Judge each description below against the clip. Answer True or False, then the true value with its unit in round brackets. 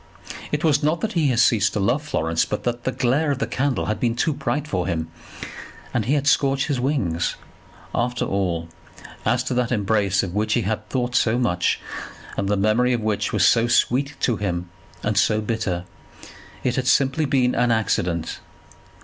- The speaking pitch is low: True (120 Hz)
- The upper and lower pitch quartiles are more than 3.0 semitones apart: True (4.5 semitones)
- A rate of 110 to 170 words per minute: False (190 wpm)